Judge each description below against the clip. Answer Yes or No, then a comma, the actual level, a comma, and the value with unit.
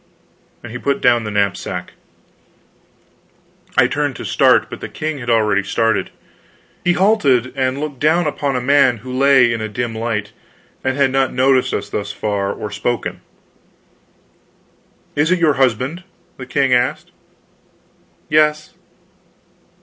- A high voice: No, low, 130 Hz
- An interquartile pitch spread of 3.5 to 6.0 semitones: Yes, average, 3.8 semitones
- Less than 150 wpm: Yes, average, 140 wpm